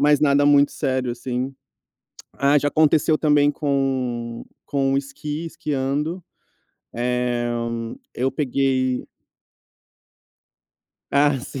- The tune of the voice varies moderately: No, narrow, 2.2 semitones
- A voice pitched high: No, medium, 140 Hz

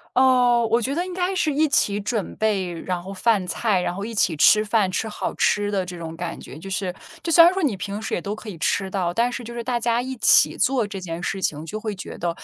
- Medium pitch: No, high, 210 Hz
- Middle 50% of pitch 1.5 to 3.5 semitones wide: No, average, 4.5 semitones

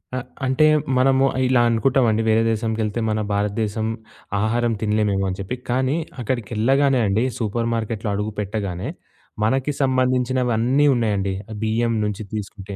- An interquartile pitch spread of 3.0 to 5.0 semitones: Yes, average, 3.3 semitones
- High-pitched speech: No, low, 115 Hz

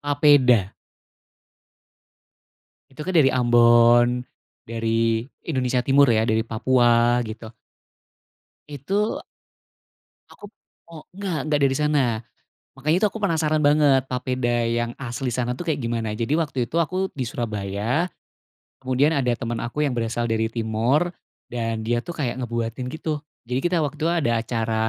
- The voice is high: No, low, 125 Hz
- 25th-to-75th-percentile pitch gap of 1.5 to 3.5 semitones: No, average, 4.1 semitones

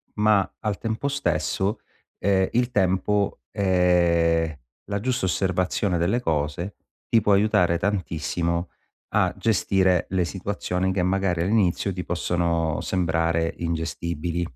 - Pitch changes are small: No, average, 3.0 semitones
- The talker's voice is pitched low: Yes, very low, 90 Hz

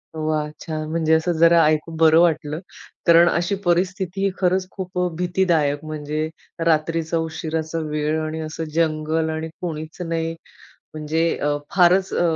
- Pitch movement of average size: No, narrow, 1.8 semitones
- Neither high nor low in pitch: Yes, medium, 160 Hz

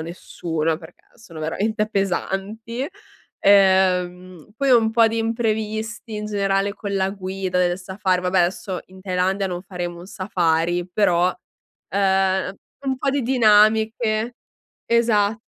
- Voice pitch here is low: No, high, 195 Hz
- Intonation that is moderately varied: Yes, average, 3.2 semitones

